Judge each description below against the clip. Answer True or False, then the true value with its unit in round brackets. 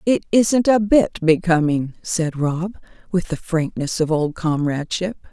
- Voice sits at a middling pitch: True (175 Hz)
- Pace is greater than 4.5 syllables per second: False (4.2 syllables/s)